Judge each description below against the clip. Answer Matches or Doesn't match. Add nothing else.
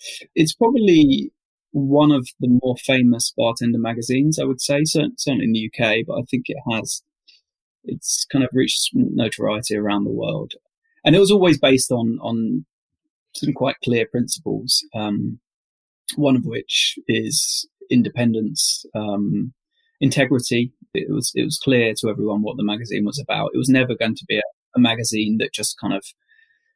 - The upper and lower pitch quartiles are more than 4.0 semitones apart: Matches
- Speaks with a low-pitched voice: Matches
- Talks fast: Doesn't match